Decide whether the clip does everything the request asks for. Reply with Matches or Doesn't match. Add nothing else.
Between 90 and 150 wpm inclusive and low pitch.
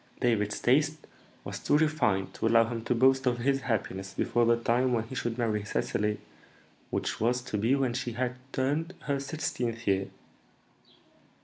Doesn't match